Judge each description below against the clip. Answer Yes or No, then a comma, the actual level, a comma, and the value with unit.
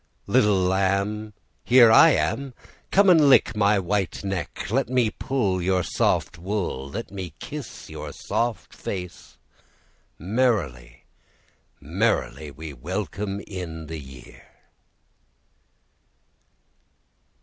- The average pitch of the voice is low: Yes, low, 100 Hz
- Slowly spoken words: Yes, slow, 105 wpm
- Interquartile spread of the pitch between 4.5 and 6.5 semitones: Yes, average, 4.9 semitones